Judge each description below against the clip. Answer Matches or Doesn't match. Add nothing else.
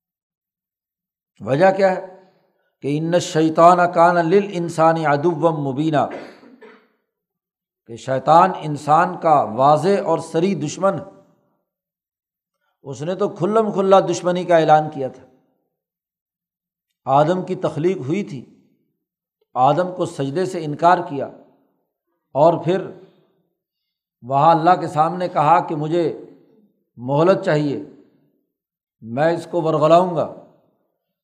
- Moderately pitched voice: Matches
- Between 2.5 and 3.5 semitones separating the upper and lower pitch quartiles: Matches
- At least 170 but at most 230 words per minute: Doesn't match